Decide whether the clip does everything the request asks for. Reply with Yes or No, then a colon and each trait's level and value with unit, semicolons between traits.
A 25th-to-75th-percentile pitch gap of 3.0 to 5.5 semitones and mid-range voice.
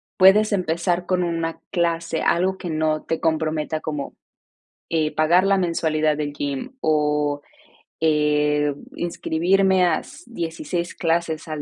No: narrow, 2.5 semitones; medium, 165 Hz